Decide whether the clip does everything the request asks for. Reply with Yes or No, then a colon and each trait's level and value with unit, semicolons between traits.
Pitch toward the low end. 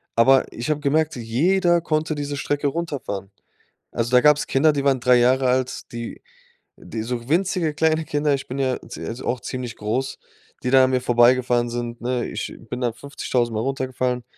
Yes: low, 130 Hz